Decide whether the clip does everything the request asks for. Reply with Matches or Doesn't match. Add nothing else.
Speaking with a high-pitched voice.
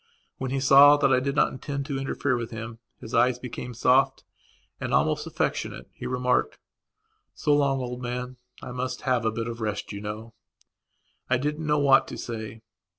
Doesn't match